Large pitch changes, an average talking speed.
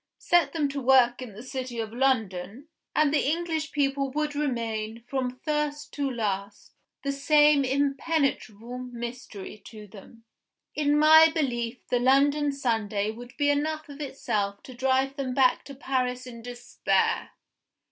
No: average, 3.6 semitones; average, 145 wpm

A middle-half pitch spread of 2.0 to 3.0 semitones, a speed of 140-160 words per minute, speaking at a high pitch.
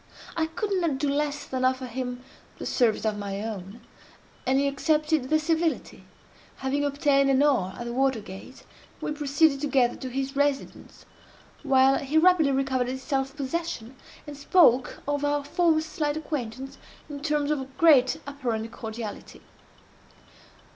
Yes: narrow, 2.6 semitones; average, 150 wpm; very high, 275 Hz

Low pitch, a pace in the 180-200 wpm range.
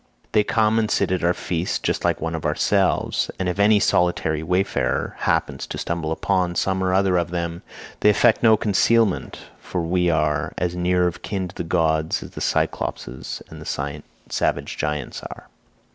Yes: very low, 90 Hz; average, 190 wpm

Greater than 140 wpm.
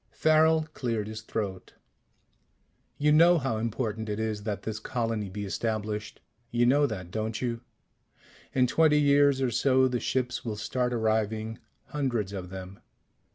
Yes: average, 150 wpm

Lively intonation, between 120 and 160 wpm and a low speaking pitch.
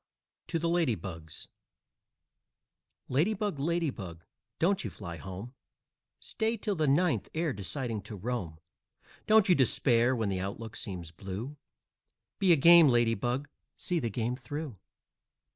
Yes: wide, 8.6 semitones; average, 145 wpm; low, 125 Hz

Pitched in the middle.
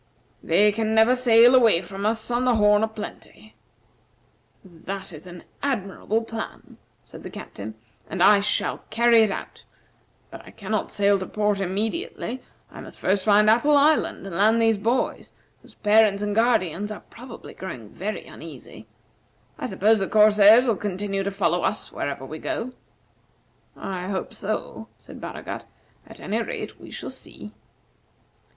No: high, 210 Hz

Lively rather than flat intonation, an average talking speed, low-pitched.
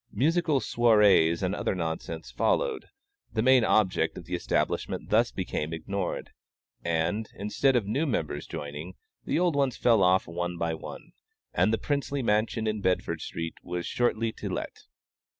Yes: wide, 6.1 semitones; average, 155 wpm; low, 100 Hz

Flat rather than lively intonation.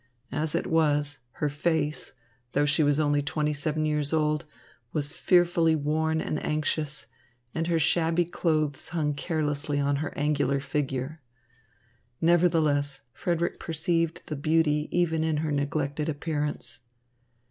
Yes: narrow, 1.8 semitones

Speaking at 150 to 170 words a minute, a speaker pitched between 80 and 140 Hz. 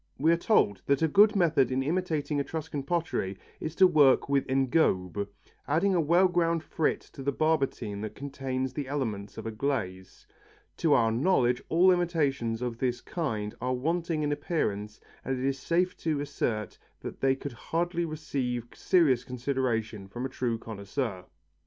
Yes: average, 165 wpm; low, 135 Hz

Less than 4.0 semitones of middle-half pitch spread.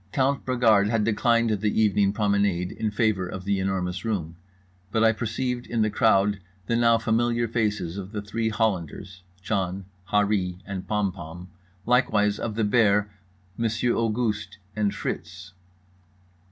Yes: average, 2.9 semitones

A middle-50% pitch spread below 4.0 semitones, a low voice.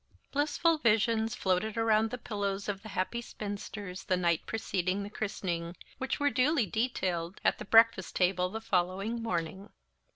No: average, 3.6 semitones; high, 205 Hz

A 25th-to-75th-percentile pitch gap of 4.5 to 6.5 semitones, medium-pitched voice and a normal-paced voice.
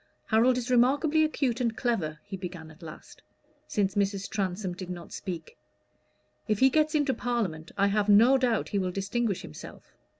No: average, 5.0 semitones; high, 205 Hz; average, 170 wpm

